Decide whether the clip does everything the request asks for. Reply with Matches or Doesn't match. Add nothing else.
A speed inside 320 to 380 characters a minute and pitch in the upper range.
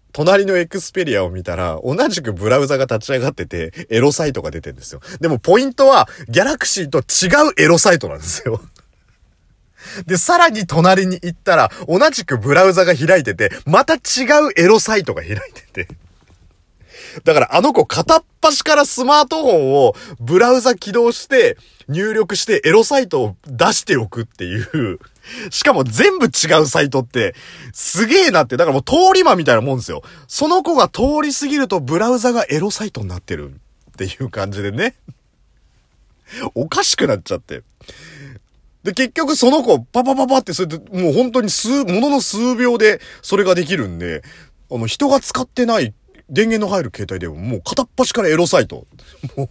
Matches